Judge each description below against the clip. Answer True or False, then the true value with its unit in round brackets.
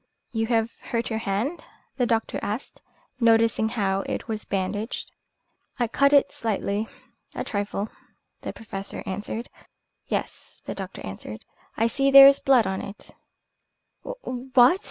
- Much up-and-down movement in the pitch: False (3.5 semitones)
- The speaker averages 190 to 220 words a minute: False (135 wpm)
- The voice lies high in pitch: True (225 Hz)